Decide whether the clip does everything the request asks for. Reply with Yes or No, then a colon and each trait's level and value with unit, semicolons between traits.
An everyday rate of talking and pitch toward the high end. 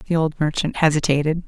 No: average, 165 wpm; medium, 155 Hz